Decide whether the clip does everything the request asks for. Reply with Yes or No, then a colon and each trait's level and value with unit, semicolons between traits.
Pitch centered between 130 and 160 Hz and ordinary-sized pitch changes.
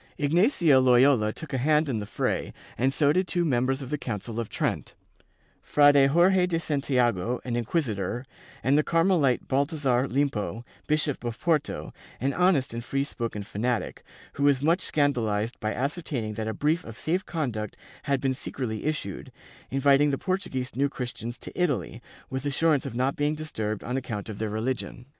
Yes: low, 135 Hz; average, 4.2 semitones